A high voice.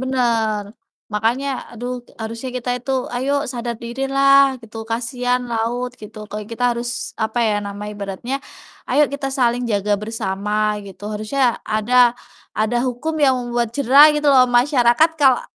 Yes: high, 240 Hz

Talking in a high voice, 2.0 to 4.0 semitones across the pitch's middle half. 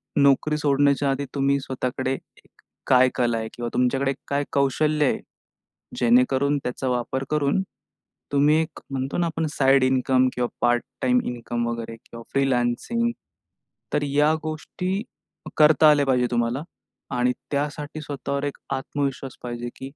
No: low, 135 Hz; average, 2.7 semitones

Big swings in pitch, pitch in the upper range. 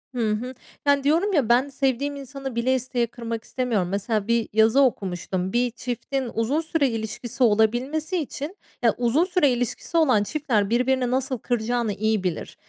No: average, 3.8 semitones; high, 245 Hz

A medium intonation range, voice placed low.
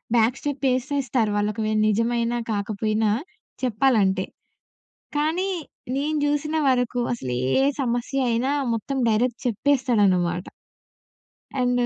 No: average, 4.1 semitones; high, 235 Hz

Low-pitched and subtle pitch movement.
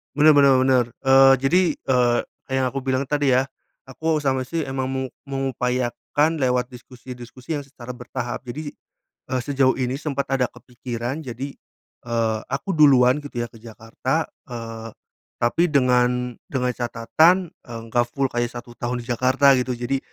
Yes: low, 130 Hz; narrow, 2.2 semitones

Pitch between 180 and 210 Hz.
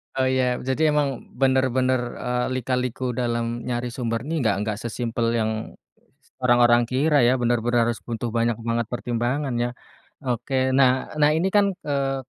No: low, 125 Hz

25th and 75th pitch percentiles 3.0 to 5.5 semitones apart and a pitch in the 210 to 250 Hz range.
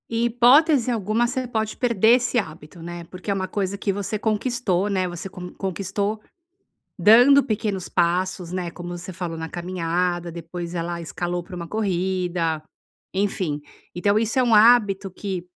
No: average, 3.9 semitones; high, 190 Hz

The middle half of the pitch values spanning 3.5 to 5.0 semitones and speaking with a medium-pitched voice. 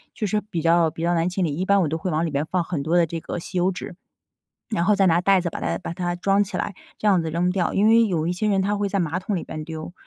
No: average, 2.9 semitones; medium, 180 Hz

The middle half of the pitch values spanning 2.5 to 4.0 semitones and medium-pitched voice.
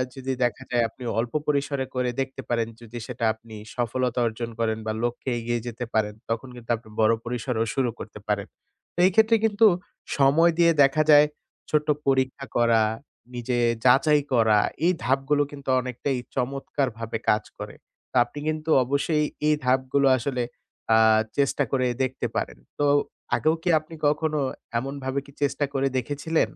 No: average, 3.4 semitones; low, 130 Hz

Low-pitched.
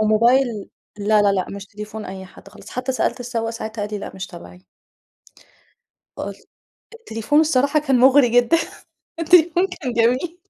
No: high, 235 Hz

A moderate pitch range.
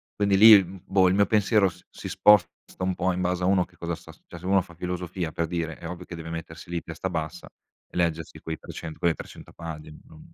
No: narrow, 2.2 semitones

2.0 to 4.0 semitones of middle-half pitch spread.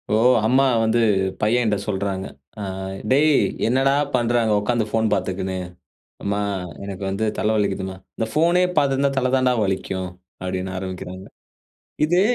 No: average, 5.1 semitones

